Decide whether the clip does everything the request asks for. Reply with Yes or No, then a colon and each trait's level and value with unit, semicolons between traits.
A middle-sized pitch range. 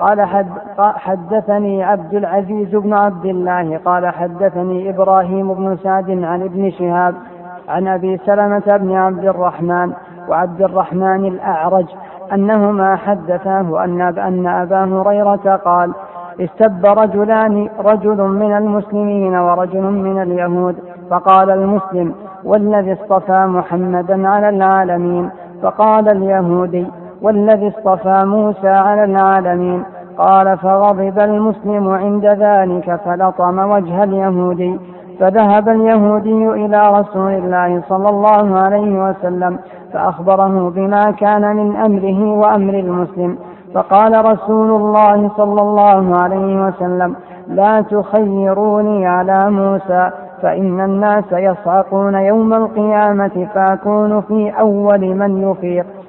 No: narrow, 2.2 semitones